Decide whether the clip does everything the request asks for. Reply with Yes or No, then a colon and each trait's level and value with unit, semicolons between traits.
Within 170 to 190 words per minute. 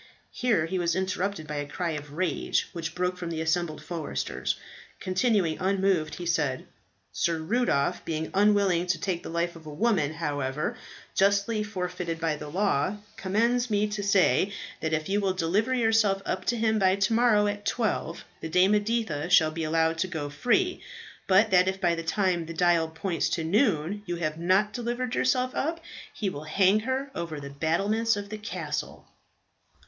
Yes: average, 180 wpm